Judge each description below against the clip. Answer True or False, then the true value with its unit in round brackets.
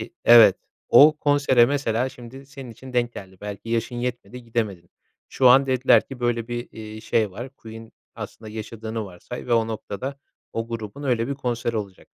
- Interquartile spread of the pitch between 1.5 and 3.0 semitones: True (2.6 semitones)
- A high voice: False (120 Hz)